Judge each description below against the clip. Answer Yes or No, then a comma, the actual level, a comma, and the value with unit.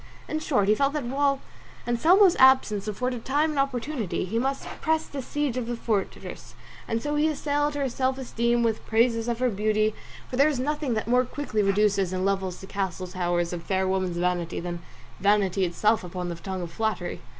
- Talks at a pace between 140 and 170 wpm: No, average, 195 wpm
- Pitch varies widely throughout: Yes, wide, 6.1 semitones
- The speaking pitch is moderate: No, high, 225 Hz